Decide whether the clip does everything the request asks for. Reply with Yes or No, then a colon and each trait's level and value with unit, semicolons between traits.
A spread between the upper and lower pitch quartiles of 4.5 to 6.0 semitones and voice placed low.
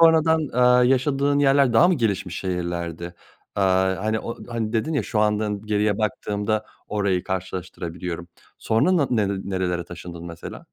Yes: average, 5.3 semitones; low, 105 Hz